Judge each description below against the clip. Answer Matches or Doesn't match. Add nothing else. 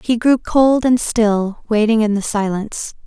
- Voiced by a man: Doesn't match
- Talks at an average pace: Matches